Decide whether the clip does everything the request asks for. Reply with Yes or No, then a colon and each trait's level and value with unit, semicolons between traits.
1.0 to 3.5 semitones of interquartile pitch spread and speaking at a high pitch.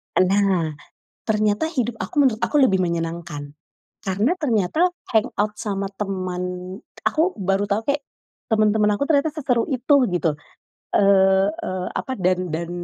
No: average, 4.7 semitones; high, 205 Hz